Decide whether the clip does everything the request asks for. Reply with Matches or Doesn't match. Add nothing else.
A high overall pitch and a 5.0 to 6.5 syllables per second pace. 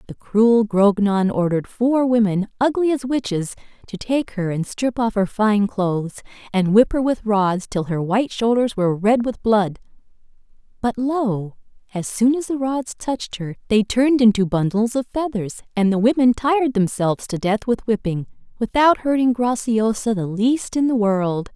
Doesn't match